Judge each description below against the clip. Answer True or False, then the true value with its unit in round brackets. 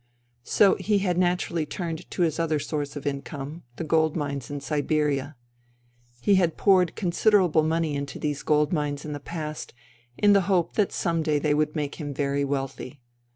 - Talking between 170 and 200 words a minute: True (195 wpm)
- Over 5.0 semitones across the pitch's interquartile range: False (3.1 semitones)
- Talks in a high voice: False (155 Hz)